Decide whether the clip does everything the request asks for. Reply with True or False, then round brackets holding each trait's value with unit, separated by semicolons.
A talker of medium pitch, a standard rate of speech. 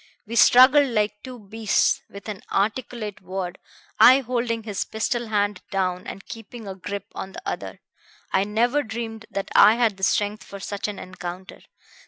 False (210 Hz; 170 wpm)